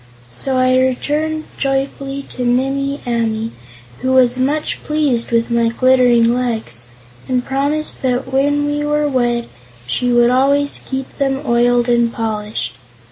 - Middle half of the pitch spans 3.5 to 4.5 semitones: No, narrow, 2.6 semitones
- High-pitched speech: Yes, very high, 255 Hz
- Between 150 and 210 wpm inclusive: No, slow, 135 wpm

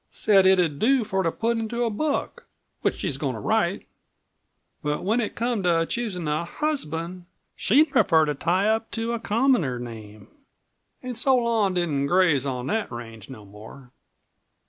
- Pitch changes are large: Yes, wide, 7.5 semitones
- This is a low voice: No, medium, 185 Hz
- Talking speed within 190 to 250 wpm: No, average, 170 wpm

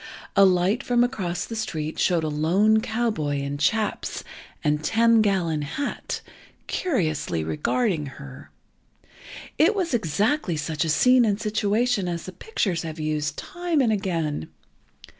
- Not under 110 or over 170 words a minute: Yes, average, 140 wpm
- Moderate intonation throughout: No, wide, 6.8 semitones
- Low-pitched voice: No, medium, 185 Hz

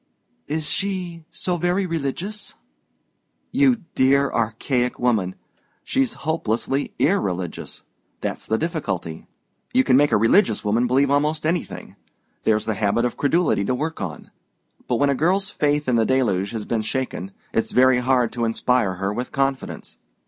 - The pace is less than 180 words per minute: Yes, average, 150 wpm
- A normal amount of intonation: No, wide, 6.0 semitones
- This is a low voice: Yes, low, 130 Hz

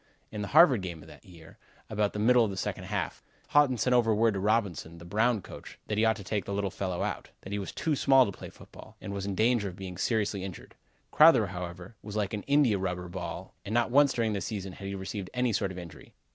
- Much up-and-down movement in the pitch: No, average, 3.2 semitones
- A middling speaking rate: No, fast, 255 wpm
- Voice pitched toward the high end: No, low, 100 Hz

